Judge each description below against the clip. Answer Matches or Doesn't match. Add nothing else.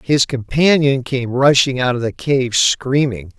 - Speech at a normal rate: Matches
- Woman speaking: Doesn't match